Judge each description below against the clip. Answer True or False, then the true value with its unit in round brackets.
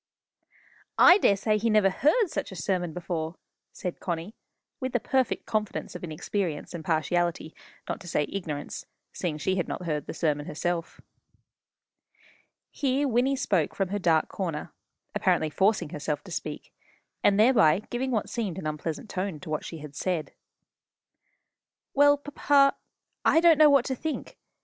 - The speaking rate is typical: True (155 wpm)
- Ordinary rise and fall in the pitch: False (7.3 semitones)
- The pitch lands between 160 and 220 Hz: True (185 Hz)